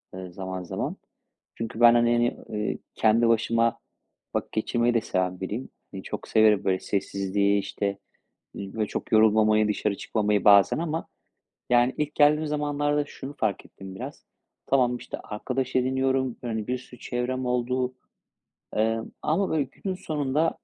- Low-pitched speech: Yes, low, 115 Hz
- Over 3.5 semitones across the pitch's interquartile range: Yes, average, 4.0 semitones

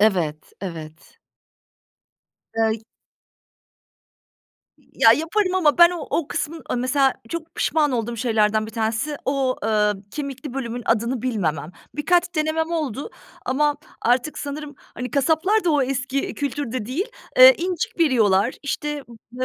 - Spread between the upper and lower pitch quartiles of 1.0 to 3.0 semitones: No, average, 5.3 semitones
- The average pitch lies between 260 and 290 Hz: Yes, very high, 270 Hz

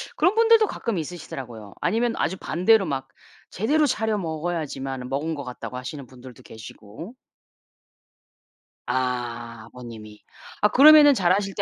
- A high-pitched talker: No, medium, 155 Hz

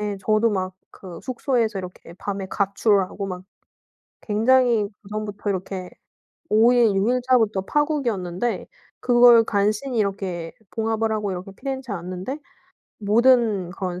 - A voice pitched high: Yes, high, 210 Hz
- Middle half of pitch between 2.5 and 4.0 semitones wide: Yes, average, 3.7 semitones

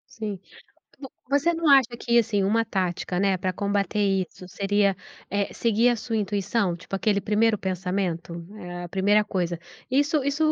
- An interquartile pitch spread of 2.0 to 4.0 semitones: Yes, average, 3.5 semitones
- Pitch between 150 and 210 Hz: Yes, high, 205 Hz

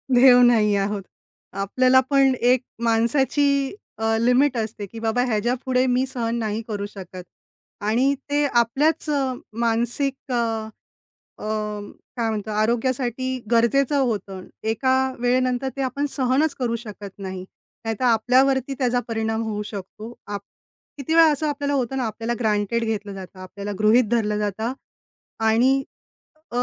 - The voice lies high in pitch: Yes, high, 235 Hz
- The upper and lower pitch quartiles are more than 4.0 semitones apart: No, average, 3.3 semitones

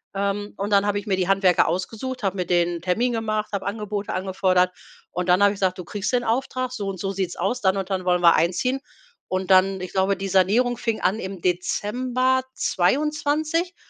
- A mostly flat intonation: No, average, 3.6 semitones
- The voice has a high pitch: Yes, high, 195 Hz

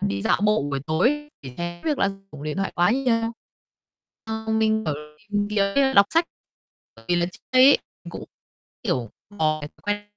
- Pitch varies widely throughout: Yes, wide, 6.5 semitones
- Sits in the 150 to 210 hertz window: Yes, high, 200 Hz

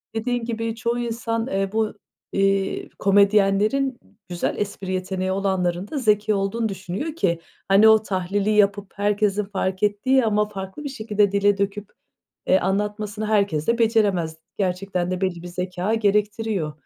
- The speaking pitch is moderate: No, high, 205 Hz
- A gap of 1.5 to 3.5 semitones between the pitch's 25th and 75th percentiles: Yes, narrow, 2.4 semitones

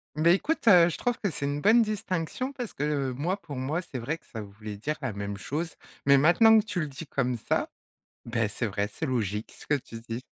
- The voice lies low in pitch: No, medium, 145 Hz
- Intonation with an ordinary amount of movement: No, wide, 7.2 semitones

